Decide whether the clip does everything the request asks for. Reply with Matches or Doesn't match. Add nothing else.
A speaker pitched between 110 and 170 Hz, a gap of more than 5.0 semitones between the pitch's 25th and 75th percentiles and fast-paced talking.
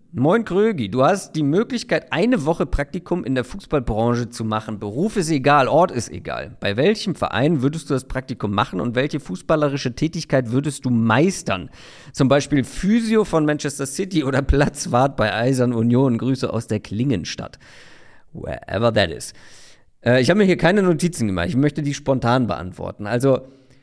Doesn't match